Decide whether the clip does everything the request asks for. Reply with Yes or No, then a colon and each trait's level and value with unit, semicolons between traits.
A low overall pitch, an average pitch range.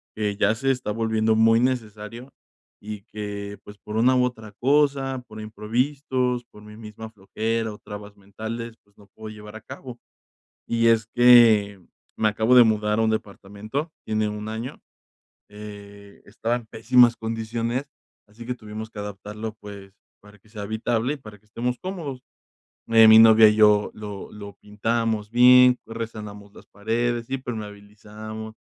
No: low, 110 Hz; narrow, 2.2 semitones